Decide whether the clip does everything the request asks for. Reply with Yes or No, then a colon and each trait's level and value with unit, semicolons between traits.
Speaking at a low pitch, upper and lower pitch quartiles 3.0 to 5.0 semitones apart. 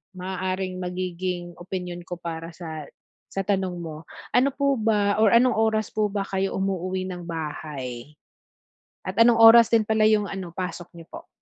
No: medium, 185 Hz; average, 3.5 semitones